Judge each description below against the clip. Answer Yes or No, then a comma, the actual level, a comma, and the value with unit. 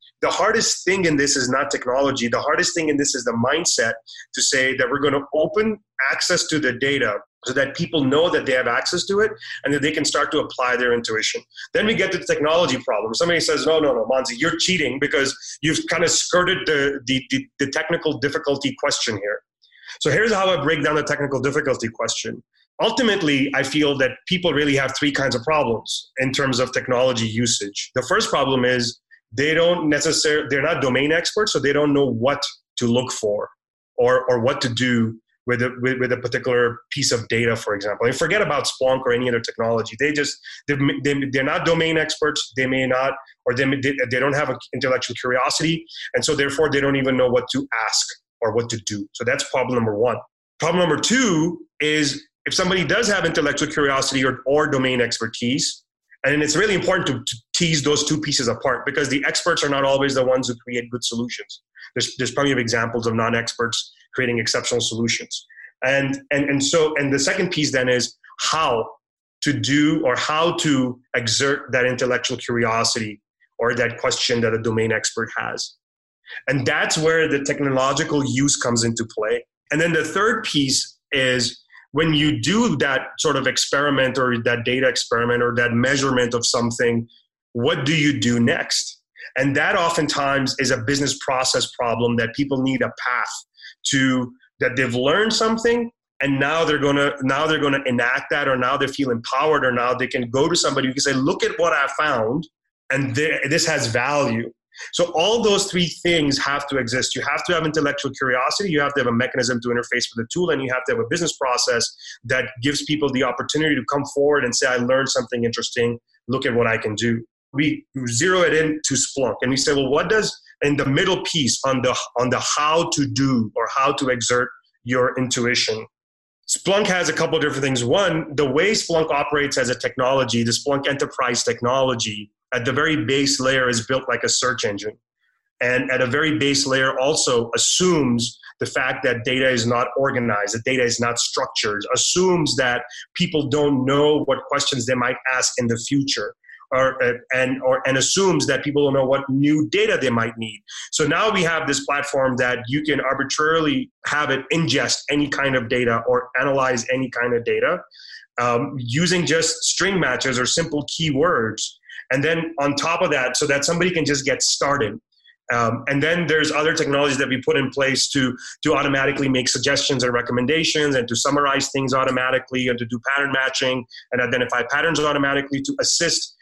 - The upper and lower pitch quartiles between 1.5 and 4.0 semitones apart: Yes, average, 3.4 semitones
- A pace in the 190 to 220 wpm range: Yes, average, 195 wpm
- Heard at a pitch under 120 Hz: No, medium, 140 Hz